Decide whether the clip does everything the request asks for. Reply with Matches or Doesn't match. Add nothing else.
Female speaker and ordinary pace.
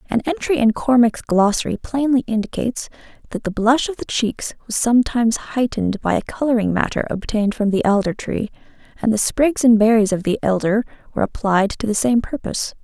Matches